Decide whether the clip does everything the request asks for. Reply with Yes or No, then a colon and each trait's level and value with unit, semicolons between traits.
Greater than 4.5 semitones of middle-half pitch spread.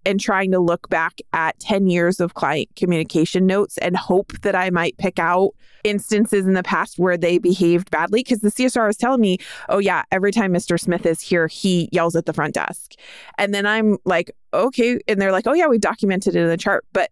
No: average, 2.9 semitones